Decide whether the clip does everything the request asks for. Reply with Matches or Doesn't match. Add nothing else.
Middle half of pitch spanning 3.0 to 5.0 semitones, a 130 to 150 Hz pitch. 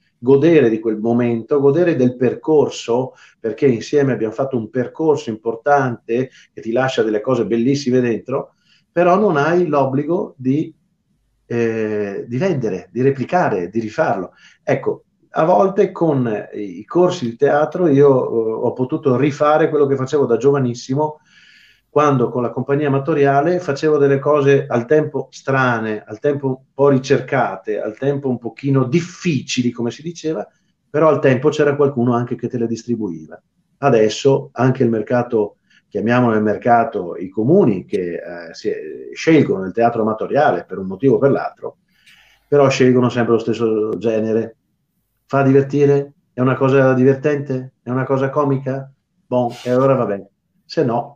Matches